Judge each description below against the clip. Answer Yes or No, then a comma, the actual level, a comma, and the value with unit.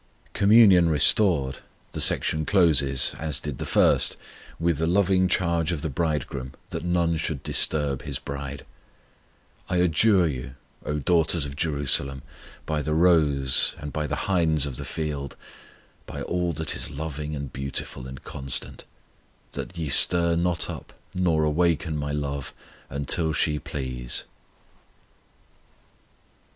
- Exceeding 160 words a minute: No, average, 140 wpm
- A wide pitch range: No, average, 3.4 semitones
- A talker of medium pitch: No, very low, 75 Hz